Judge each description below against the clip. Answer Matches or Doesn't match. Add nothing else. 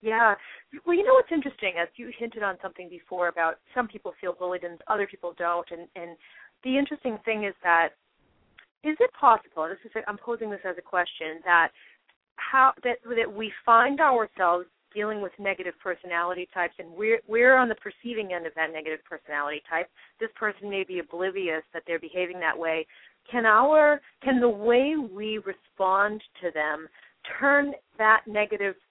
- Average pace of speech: Matches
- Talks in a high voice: Matches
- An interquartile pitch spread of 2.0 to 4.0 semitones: Doesn't match